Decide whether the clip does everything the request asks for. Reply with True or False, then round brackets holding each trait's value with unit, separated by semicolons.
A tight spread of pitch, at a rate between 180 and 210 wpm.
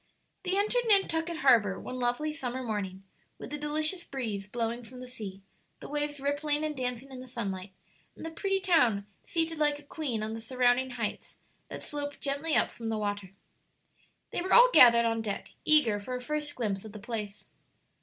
False (5.3 semitones; 190 wpm)